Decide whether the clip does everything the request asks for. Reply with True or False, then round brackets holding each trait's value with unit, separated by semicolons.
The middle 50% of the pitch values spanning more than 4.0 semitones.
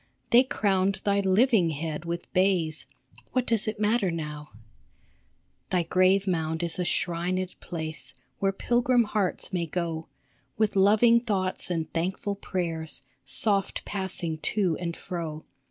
False (3.5 semitones)